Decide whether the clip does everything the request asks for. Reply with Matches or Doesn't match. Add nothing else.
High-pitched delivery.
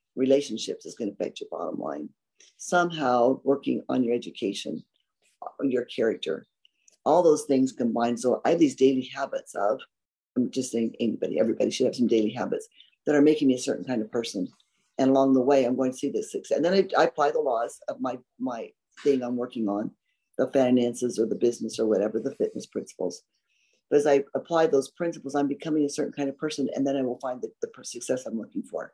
Doesn't match